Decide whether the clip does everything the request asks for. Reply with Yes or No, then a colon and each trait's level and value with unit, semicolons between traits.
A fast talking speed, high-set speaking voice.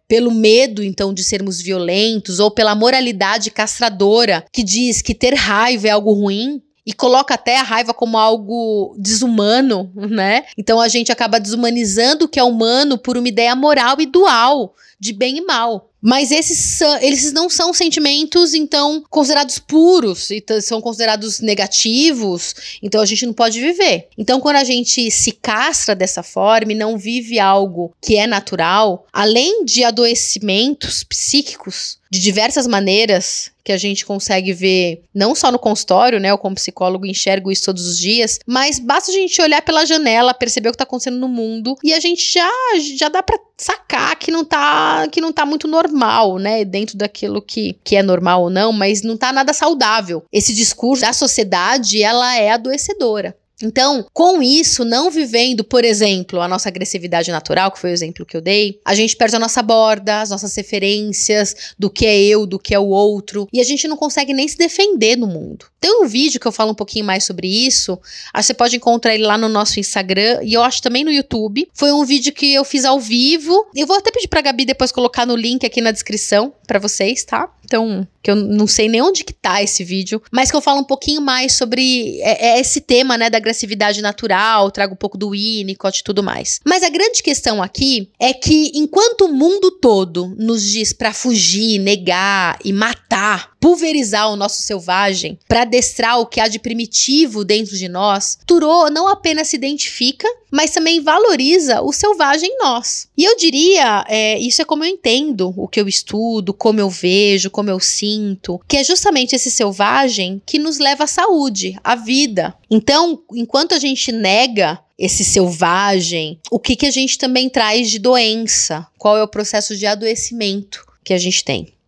Yes: fast, 190 wpm; high, 230 Hz